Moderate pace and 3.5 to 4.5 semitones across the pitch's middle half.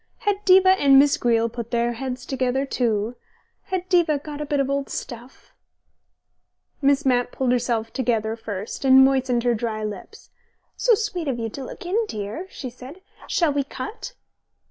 Yes: average, 170 wpm; average, 4.1 semitones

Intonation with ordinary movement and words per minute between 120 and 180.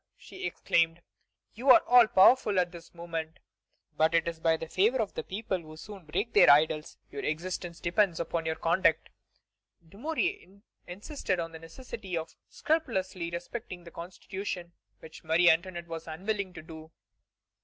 Yes: average, 3.6 semitones; average, 155 wpm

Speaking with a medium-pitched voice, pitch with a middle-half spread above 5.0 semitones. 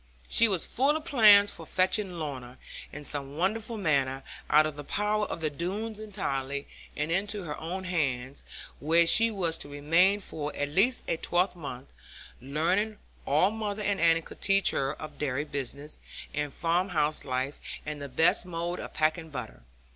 Yes: medium, 165 Hz; wide, 5.4 semitones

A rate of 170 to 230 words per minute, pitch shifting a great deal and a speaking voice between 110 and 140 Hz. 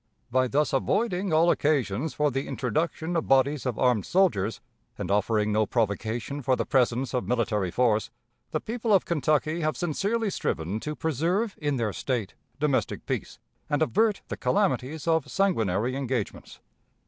No: average, 155 wpm; wide, 5.8 semitones; low, 135 Hz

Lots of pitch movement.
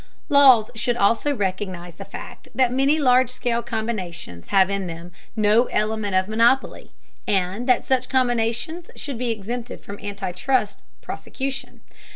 No: average, 4.2 semitones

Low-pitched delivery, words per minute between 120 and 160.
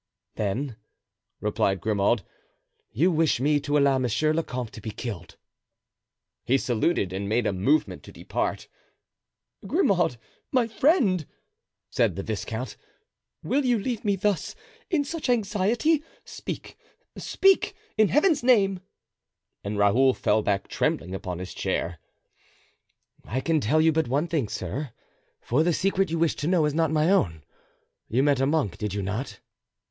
No: medium, 145 Hz; average, 150 wpm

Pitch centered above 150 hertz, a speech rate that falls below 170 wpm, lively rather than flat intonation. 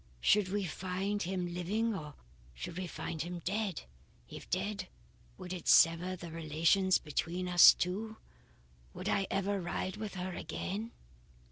No: medium, 185 Hz; average, 145 wpm; narrow, 2.5 semitones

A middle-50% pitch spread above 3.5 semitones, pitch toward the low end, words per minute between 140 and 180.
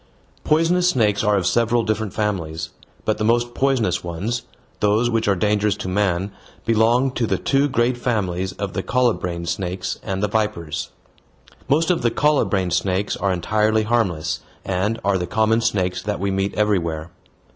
Yes: average, 3.9 semitones; low, 105 Hz; average, 165 wpm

